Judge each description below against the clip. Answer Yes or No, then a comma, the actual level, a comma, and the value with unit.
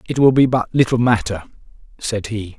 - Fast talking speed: No, average, 185 wpm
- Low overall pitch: Yes, low, 115 Hz